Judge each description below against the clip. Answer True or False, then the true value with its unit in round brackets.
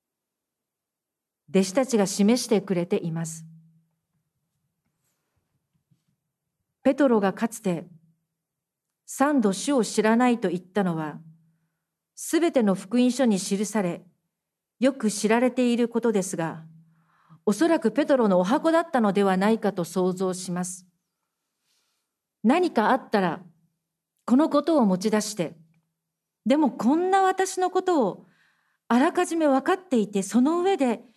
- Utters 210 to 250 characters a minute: True (240 characters per minute)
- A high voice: True (205 Hz)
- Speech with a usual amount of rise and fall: False (7.1 semitones)